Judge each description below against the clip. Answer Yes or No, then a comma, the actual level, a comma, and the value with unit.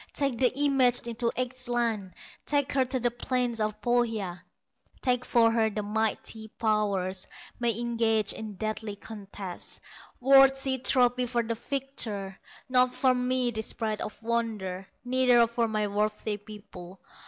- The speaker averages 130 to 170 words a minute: Yes, average, 140 wpm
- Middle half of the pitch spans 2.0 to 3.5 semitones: Yes, average, 2.9 semitones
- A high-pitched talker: Yes, high, 230 Hz